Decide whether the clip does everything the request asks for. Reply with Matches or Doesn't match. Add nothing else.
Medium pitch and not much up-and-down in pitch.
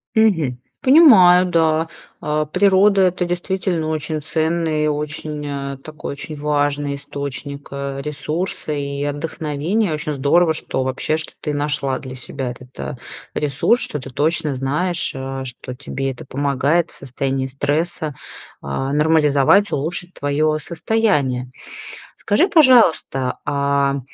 Doesn't match